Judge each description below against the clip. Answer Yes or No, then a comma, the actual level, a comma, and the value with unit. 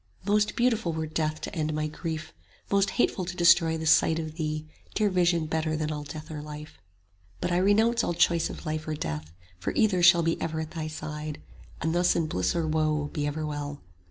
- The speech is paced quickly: Yes, fast, 215 wpm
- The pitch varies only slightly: Yes, narrow, 2.2 semitones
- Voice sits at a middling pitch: Yes, medium, 160 Hz